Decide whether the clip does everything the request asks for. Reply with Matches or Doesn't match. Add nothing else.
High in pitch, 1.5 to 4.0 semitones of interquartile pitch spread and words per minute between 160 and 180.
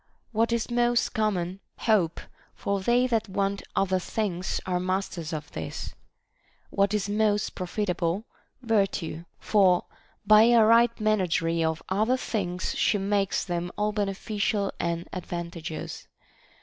Doesn't match